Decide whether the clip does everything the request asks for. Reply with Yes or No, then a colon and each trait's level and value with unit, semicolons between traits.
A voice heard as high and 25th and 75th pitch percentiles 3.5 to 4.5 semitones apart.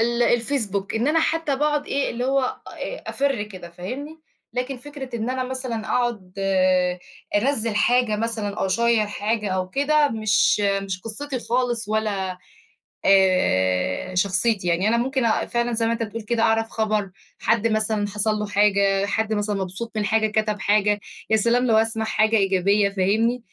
No: high, 220 Hz; average, 3.0 semitones